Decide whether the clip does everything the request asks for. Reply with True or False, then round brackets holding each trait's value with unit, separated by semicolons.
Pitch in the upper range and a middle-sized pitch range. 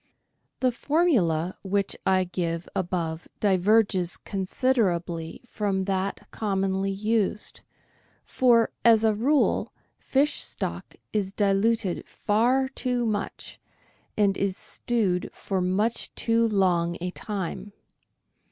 True (200 Hz; 3.6 semitones)